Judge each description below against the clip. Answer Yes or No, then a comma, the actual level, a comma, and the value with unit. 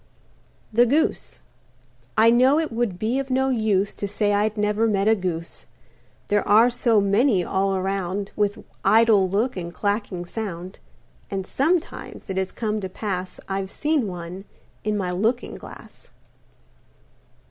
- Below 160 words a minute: Yes, average, 145 wpm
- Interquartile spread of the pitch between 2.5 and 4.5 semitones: Yes, average, 3.3 semitones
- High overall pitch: Yes, high, 205 Hz